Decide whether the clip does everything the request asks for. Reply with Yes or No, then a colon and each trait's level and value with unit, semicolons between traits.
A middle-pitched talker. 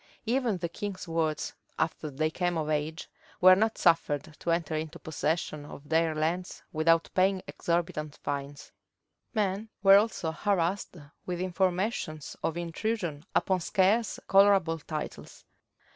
Yes: medium, 170 Hz